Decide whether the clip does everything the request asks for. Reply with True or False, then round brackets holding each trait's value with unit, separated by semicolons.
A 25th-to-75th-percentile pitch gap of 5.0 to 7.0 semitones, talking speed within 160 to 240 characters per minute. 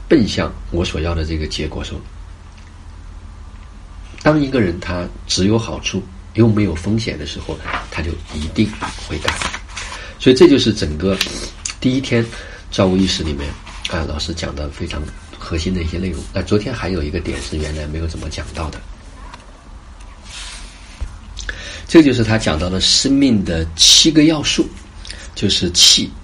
False (3.8 semitones; 225 characters per minute)